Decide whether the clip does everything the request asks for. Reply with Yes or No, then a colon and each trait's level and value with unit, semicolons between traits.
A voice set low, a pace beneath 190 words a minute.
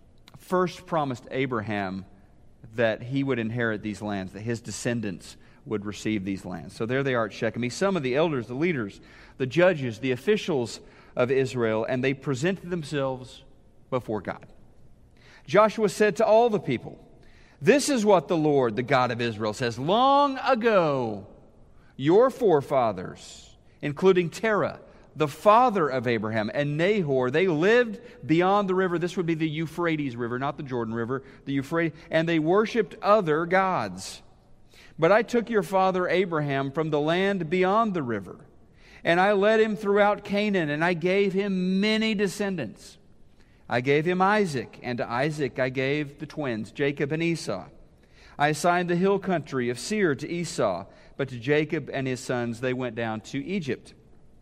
No: medium, 145 Hz; average, 165 wpm